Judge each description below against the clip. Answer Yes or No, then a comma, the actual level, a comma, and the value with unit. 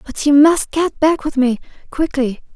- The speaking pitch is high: Yes, very high, 285 Hz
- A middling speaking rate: Yes, average, 190 wpm